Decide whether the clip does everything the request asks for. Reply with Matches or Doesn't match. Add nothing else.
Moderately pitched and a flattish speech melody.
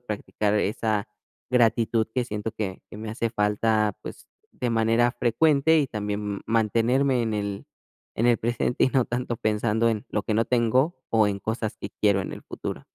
Doesn't match